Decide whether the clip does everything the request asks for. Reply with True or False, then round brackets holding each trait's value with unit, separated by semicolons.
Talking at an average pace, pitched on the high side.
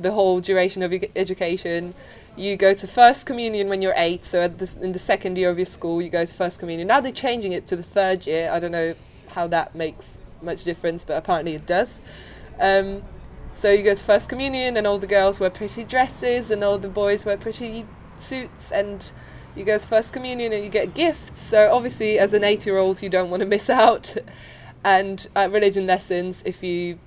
False (215 wpm; 195 Hz)